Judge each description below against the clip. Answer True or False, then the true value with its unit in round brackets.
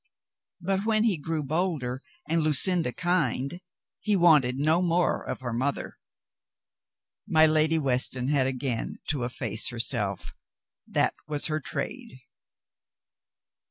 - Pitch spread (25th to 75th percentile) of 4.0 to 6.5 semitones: True (5.0 semitones)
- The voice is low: False (150 Hz)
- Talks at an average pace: False (125 wpm)